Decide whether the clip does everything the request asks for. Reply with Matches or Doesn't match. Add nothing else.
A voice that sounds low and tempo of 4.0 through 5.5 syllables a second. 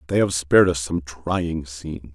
Matches